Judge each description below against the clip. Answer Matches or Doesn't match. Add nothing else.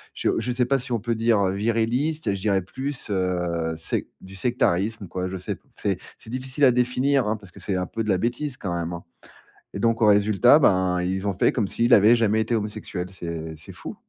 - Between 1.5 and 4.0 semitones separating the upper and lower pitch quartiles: Doesn't match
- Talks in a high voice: Doesn't match